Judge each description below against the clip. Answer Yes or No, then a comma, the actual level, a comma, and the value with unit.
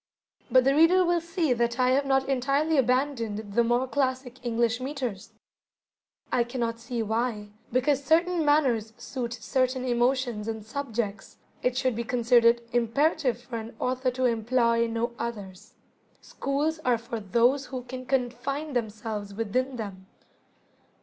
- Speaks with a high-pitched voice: Yes, high, 245 Hz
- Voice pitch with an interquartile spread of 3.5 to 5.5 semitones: No, narrow, 2.6 semitones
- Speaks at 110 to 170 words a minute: Yes, average, 145 wpm